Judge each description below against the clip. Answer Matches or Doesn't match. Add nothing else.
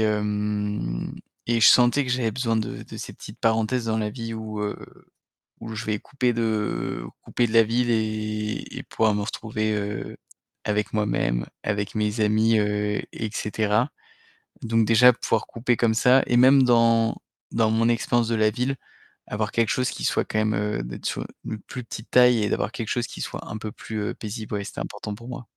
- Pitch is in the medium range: Doesn't match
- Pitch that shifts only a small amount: Matches